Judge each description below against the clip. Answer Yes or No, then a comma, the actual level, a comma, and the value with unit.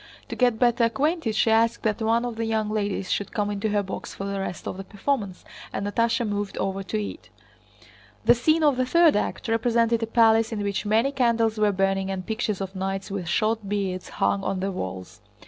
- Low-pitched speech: No, high, 215 Hz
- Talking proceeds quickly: Yes, fast, 215 wpm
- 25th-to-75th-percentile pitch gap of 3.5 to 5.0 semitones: No, average, 2.8 semitones